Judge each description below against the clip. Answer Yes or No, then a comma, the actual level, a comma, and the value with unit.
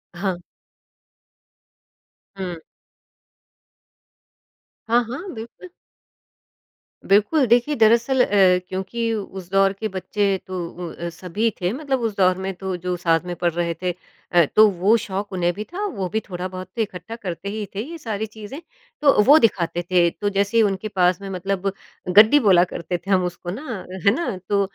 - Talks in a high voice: Yes, high, 195 Hz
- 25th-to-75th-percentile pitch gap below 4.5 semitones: Yes, average, 3.6 semitones